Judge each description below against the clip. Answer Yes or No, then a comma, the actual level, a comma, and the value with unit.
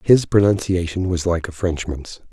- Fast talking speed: No, average, 155 wpm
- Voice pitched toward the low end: Yes, very low, 90 Hz